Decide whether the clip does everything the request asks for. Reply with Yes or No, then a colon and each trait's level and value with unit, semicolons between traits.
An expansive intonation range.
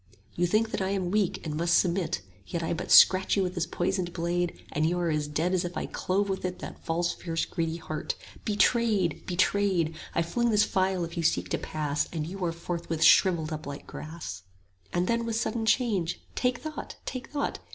No: average, 2.9 semitones